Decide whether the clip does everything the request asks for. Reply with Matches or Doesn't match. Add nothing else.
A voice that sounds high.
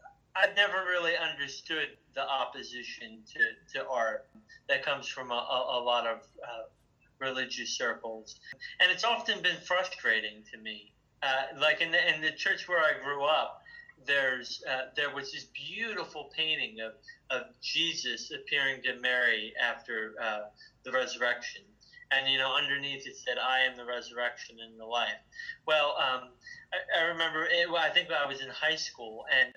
Doesn't match